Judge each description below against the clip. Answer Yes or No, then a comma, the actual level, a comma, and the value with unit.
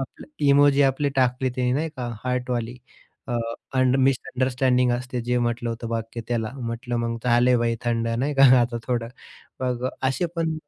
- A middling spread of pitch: No, narrow, 1.7 semitones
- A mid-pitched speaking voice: No, low, 125 Hz